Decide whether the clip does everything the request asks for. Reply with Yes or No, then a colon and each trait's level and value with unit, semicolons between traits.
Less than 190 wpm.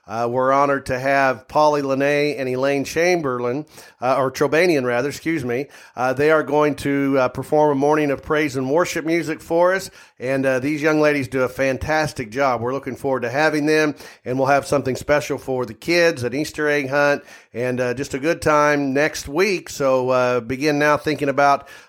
No: average, 200 wpm